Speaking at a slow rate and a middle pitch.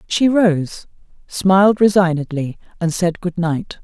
Yes: slow, 125 wpm; medium, 180 Hz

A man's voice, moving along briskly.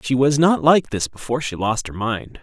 Yes: male; fast, 250 wpm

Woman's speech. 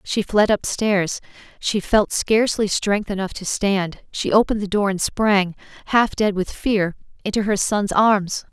Yes: female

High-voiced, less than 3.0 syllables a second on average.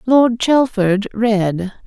Yes: high, 220 Hz; 2.6 syllables/s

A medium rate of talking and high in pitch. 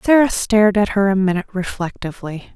Yes: average, 165 wpm; high, 200 Hz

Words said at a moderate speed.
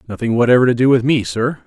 No: fast, 255 wpm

